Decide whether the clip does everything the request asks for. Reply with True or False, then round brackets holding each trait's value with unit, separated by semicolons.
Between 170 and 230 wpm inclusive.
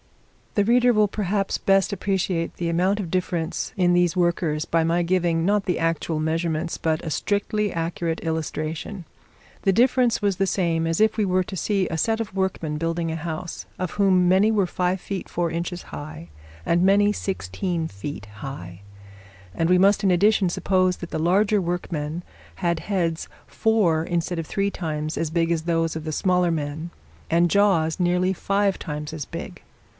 True (180 wpm)